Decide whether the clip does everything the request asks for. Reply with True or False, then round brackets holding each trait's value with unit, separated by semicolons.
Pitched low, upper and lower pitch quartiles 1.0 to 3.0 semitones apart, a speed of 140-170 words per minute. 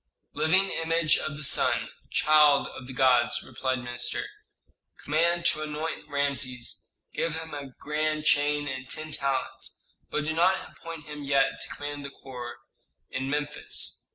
False (145 Hz; 2.6 semitones; 155 wpm)